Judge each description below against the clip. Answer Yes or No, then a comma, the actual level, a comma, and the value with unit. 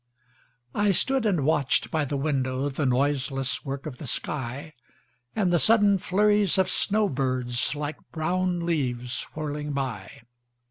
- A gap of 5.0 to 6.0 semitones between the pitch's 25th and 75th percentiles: Yes, wide, 5.4 semitones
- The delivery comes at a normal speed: No, slow, 125 wpm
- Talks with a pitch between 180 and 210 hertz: No, medium, 145 Hz